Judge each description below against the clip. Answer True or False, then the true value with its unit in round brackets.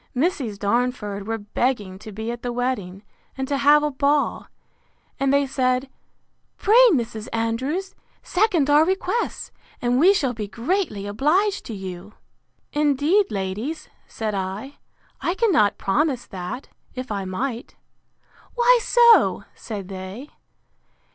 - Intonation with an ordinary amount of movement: False (6.2 semitones)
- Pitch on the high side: True (250 Hz)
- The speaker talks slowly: True (130 wpm)